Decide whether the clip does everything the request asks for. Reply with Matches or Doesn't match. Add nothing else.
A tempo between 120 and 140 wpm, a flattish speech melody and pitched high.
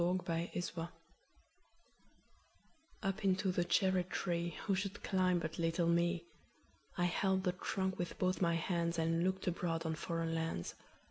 Doesn't match